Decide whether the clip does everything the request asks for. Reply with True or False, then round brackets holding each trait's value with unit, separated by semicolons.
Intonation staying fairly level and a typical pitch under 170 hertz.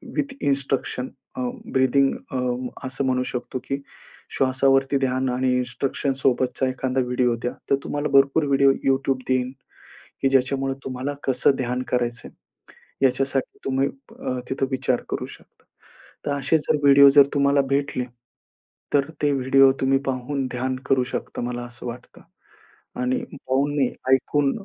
True (1.4 semitones; 135 Hz)